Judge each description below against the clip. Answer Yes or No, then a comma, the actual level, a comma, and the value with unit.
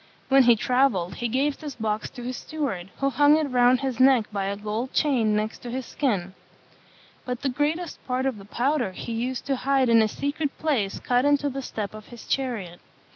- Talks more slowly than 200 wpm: No, fast, 205 wpm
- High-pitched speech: Yes, very high, 250 Hz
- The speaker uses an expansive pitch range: No, average, 4.2 semitones